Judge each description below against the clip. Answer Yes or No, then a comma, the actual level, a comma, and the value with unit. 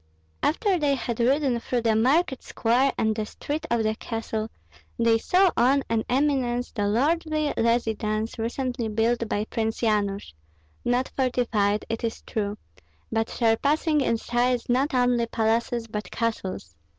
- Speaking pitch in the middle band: No, high, 235 Hz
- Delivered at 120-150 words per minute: Yes, average, 145 wpm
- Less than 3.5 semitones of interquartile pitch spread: Yes, average, 3.0 semitones